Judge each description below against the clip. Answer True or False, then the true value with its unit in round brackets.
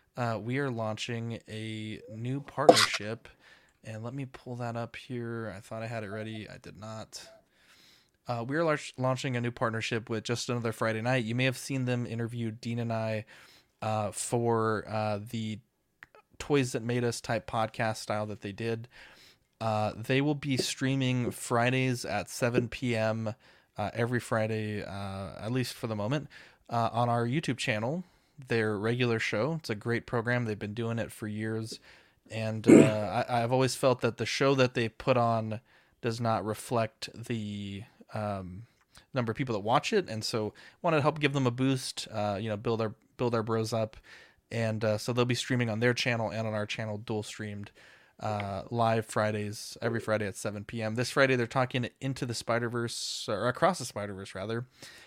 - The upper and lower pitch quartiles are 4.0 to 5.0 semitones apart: False (2.4 semitones)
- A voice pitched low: True (115 Hz)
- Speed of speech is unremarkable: True (185 wpm)